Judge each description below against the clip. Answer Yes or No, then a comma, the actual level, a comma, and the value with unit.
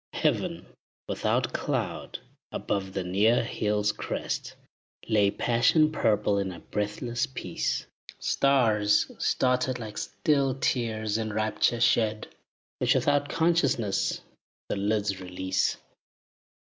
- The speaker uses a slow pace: Yes, slow, 105 wpm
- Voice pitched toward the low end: Yes, low, 110 Hz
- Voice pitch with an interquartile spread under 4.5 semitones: Yes, average, 3.3 semitones